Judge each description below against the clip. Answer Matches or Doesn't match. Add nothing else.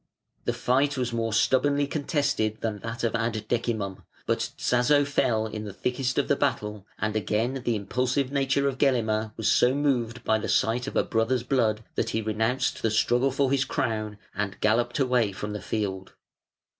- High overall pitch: Doesn't match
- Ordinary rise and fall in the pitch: Matches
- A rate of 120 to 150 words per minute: Doesn't match